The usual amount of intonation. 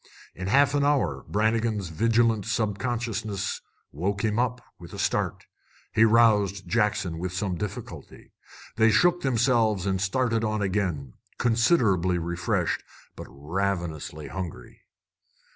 Yes: average, 3.8 semitones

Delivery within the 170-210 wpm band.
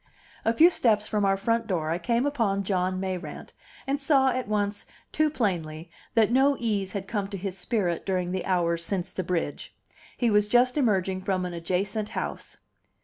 Yes: average, 185 wpm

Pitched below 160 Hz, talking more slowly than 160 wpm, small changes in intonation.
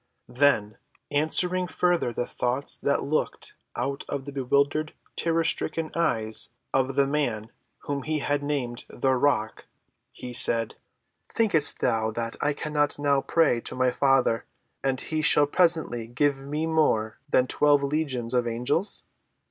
No: medium, 140 Hz; average, 140 wpm; average, 3.7 semitones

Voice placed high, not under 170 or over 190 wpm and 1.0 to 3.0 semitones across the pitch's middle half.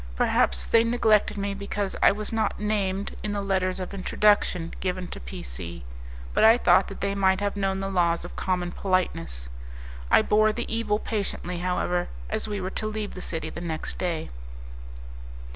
Yes: high, 195 Hz; average, 180 wpm; average, 2.7 semitones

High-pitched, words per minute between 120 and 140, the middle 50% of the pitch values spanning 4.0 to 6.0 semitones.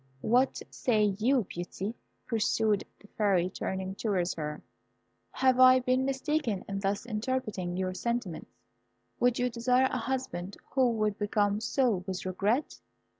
Yes: high, 215 Hz; slow, 135 wpm; average, 4.7 semitones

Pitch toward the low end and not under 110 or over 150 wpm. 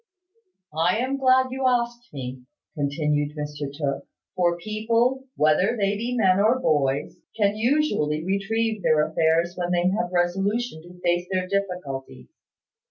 No: medium, 185 Hz; average, 140 wpm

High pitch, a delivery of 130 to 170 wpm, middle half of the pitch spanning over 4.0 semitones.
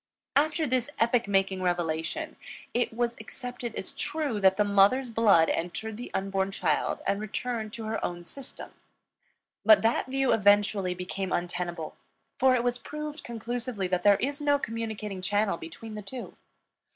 Yes: high, 220 Hz; average, 155 wpm; average, 4.4 semitones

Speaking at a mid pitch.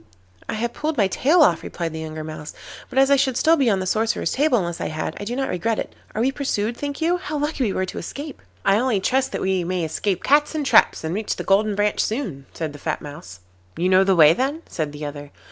No: high, 205 Hz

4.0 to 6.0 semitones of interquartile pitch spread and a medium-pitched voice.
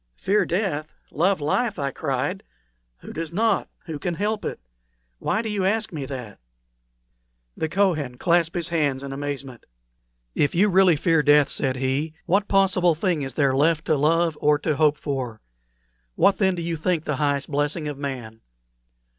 Yes: average, 4.3 semitones; medium, 155 Hz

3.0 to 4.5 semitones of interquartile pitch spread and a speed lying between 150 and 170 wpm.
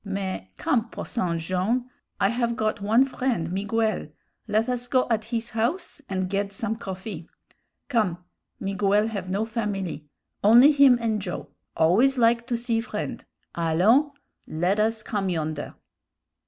No: average, 3.9 semitones; average, 140 wpm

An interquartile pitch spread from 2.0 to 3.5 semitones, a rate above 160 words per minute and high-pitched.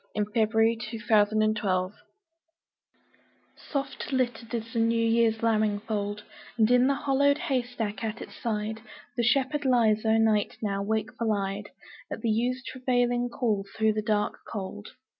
No: narrow, 2.5 semitones; average, 145 wpm; high, 225 Hz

